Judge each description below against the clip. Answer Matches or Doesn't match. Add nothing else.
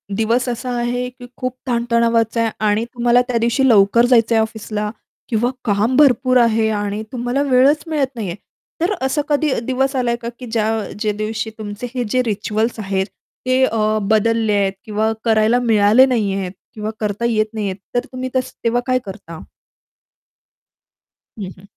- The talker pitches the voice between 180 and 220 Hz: Doesn't match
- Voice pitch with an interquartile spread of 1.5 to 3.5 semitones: Matches